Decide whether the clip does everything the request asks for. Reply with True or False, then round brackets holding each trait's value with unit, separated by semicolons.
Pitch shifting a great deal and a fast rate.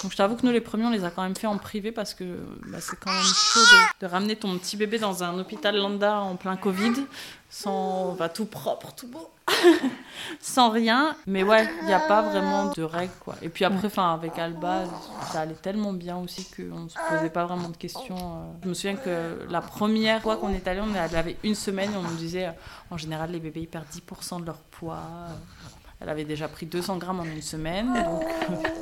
False (3.9 semitones; 230 wpm)